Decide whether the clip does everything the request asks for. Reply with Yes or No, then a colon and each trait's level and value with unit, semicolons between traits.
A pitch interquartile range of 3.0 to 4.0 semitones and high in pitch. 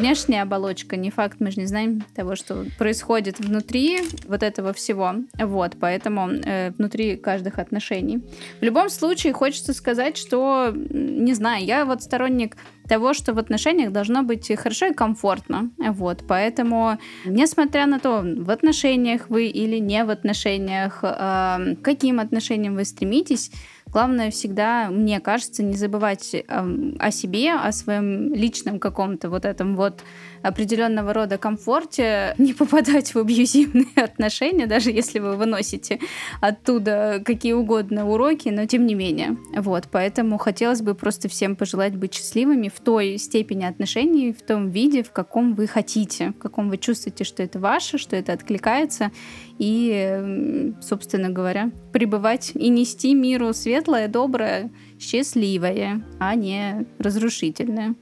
Yes: average, 3.7 semitones; high, 220 Hz